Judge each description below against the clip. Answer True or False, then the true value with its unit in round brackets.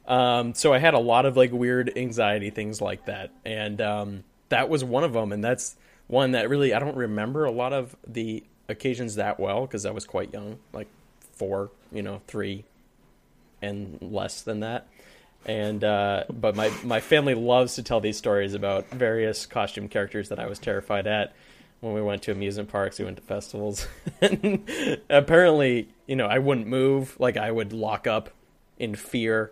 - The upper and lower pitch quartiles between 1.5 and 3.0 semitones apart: False (3.4 semitones)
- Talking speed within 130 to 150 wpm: False (190 wpm)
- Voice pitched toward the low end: True (110 Hz)